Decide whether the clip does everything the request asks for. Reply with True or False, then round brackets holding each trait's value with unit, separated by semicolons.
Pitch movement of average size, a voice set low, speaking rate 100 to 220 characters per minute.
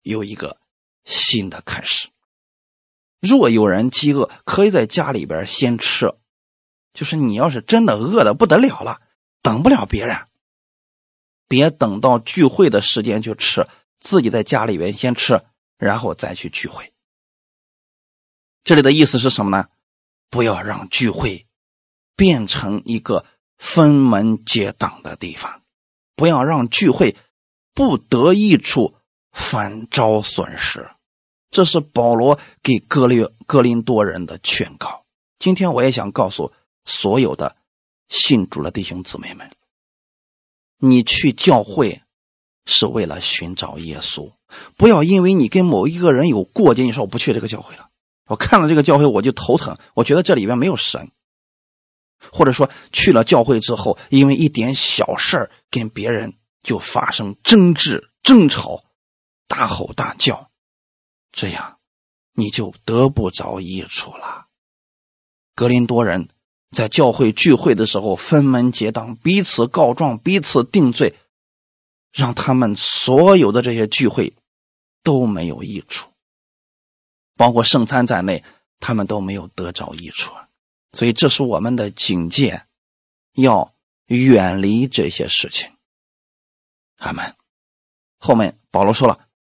False (6.4 semitones; 115 Hz; 205 characters per minute)